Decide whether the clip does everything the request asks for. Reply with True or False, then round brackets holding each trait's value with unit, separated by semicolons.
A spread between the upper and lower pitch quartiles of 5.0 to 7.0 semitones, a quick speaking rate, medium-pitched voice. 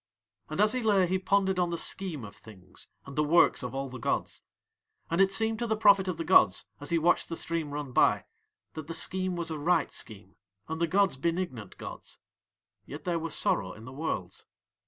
True (5.5 semitones; 215 wpm; 165 Hz)